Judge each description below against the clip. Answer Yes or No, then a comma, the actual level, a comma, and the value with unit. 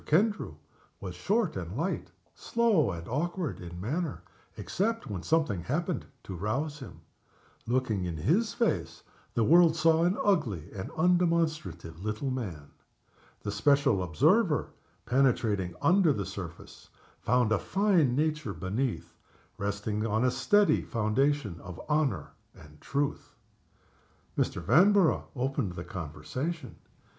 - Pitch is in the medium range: No, low, 130 Hz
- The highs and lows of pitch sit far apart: Yes, wide, 8.8 semitones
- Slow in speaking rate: Yes, slow, 125 wpm